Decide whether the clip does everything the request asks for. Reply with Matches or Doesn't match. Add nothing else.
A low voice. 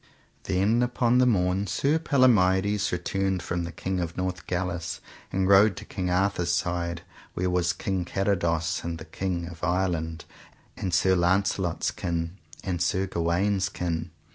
Matches